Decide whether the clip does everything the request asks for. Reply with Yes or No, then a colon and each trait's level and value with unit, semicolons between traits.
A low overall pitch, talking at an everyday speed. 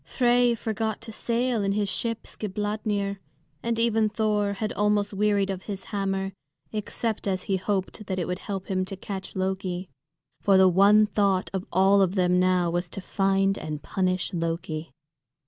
No: high, 195 Hz; average, 170 wpm